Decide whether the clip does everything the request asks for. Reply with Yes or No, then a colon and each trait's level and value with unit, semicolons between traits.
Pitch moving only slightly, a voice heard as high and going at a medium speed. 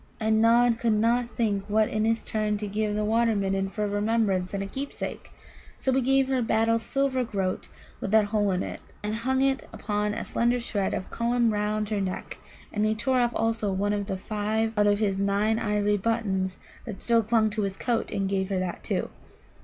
No: narrow, 2.1 semitones; high, 215 Hz; fast, 215 wpm